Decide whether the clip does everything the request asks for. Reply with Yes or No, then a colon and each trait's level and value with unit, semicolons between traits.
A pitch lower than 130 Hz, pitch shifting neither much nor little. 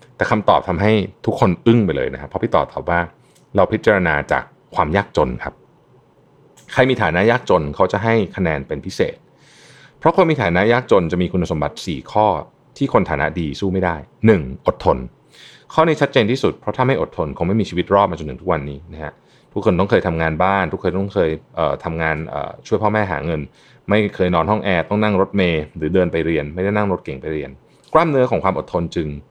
Yes: very low, 90 Hz; average, 4.3 semitones